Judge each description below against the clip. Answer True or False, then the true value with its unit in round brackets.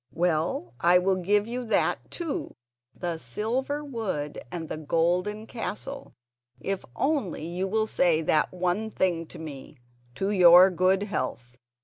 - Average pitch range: True (4.7 semitones)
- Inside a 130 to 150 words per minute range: True (140 wpm)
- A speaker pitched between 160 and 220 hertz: True (185 Hz)